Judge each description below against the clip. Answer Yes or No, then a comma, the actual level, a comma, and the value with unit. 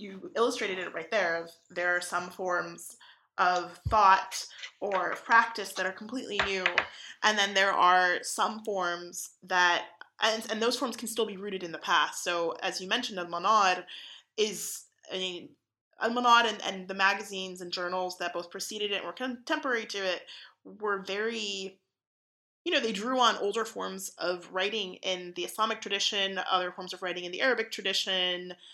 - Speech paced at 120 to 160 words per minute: No, average, 175 wpm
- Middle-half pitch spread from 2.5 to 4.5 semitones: Yes, average, 3.5 semitones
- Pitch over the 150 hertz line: Yes, high, 190 Hz